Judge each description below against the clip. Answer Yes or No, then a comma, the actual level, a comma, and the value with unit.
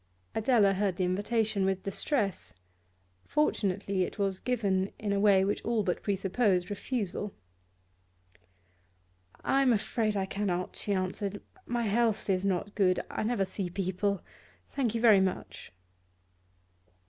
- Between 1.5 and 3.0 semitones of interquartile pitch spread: Yes, narrow, 2.5 semitones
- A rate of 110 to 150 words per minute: Yes, slow, 135 wpm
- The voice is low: No, high, 200 Hz